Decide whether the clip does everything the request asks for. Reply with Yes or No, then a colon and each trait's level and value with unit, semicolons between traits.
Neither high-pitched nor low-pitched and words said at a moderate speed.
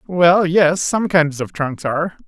Yes: medium, 165 Hz; average, 160 wpm